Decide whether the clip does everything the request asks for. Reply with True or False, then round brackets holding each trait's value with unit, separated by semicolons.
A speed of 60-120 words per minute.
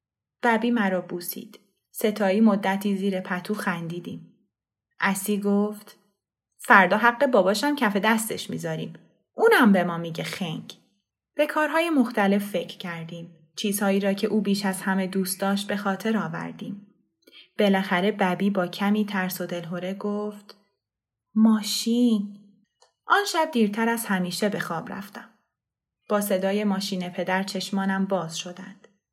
False (130 wpm)